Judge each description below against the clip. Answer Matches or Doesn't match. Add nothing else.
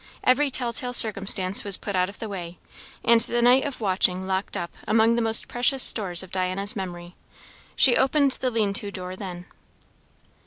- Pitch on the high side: Matches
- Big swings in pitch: Doesn't match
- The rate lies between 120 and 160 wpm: Doesn't match